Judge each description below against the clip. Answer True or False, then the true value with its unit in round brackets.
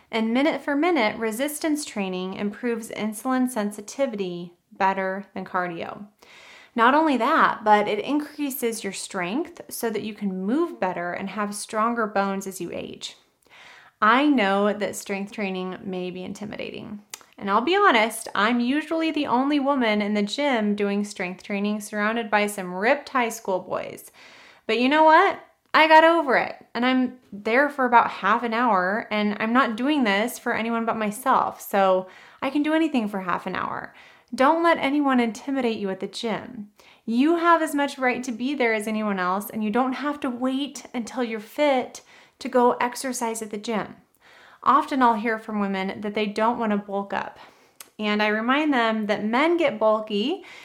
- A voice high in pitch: True (225 Hz)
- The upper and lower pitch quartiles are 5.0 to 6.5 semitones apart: False (4.4 semitones)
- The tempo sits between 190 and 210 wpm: False (180 wpm)